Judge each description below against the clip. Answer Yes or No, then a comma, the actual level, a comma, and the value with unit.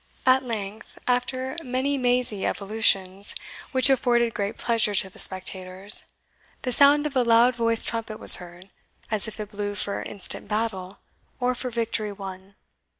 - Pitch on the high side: Yes, high, 225 Hz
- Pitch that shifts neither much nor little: Yes, average, 3.9 semitones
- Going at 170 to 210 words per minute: No, average, 150 wpm